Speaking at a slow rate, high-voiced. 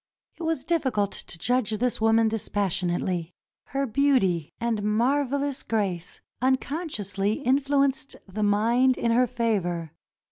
Yes: slow, 120 wpm; high, 230 Hz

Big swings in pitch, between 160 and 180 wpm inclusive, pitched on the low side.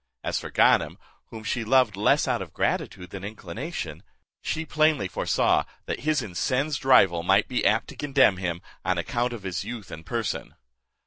Yes: wide, 6.0 semitones; average, 175 wpm; low, 110 Hz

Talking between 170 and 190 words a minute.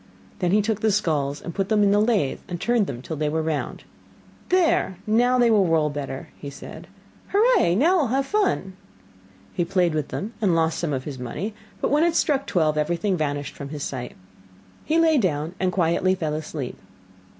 No: average, 200 wpm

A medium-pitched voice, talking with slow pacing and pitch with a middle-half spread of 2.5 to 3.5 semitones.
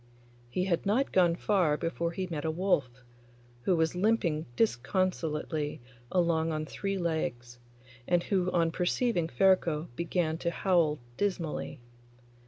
Yes: medium, 170 Hz; slow, 130 wpm; average, 2.9 semitones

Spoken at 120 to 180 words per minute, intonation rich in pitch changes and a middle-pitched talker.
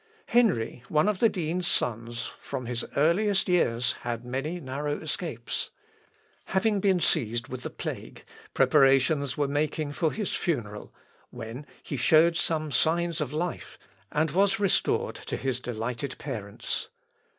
Yes: average, 140 wpm; wide, 5.7 semitones; medium, 145 Hz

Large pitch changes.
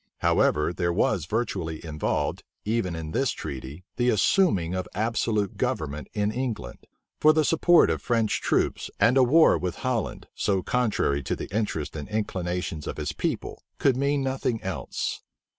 Yes: wide, 7.0 semitones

